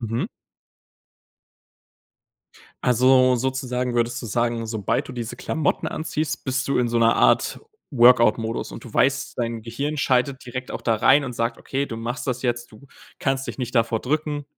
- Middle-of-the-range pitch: No, low, 125 Hz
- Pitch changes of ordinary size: No, narrow, 2.3 semitones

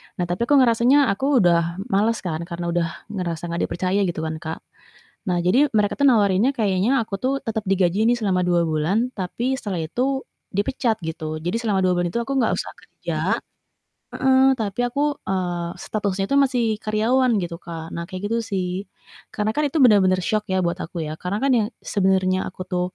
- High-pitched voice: Yes, high, 195 Hz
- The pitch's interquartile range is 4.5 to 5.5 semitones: Yes, average, 5.0 semitones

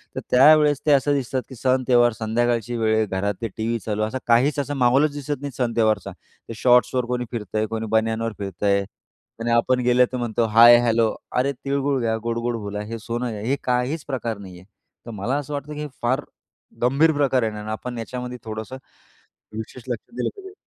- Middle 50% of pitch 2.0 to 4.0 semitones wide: Yes, average, 3.0 semitones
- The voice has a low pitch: Yes, low, 120 Hz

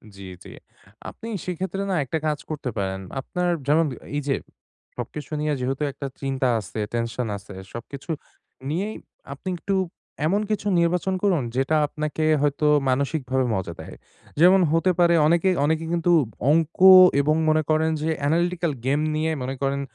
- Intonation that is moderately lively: Yes, average, 4.2 semitones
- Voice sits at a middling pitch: Yes, medium, 155 Hz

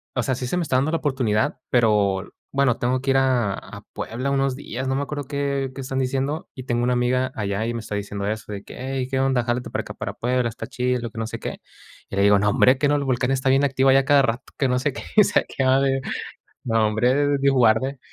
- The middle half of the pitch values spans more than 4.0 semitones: No, narrow, 2.6 semitones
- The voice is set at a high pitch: No, low, 130 Hz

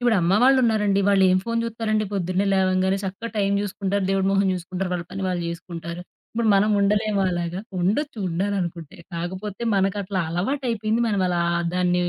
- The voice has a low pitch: No, high, 195 Hz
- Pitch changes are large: No, average, 2.8 semitones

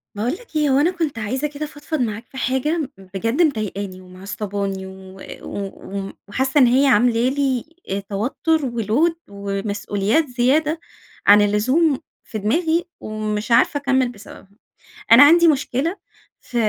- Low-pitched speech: No, high, 245 Hz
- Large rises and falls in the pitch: Yes, wide, 6.2 semitones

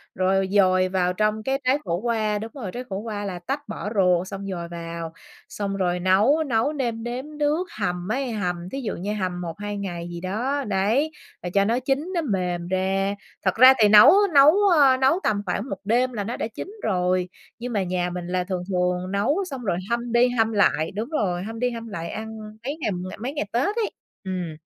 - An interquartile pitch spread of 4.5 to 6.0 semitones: Yes, average, 5.1 semitones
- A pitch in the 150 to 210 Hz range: Yes, high, 205 Hz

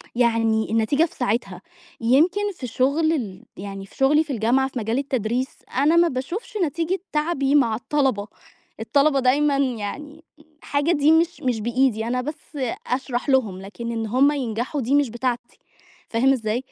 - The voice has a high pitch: Yes, very high, 260 Hz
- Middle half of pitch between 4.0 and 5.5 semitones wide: Yes, average, 4.4 semitones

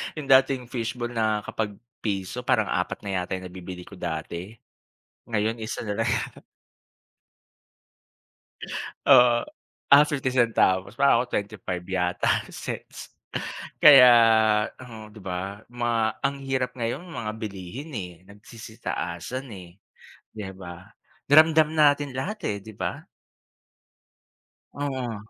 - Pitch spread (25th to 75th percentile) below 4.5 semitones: No, average, 5.0 semitones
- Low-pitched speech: Yes, low, 110 Hz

